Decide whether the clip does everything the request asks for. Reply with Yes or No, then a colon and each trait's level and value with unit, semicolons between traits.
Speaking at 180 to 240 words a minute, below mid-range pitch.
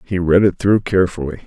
Yes: fast, 205 wpm; very low, 90 Hz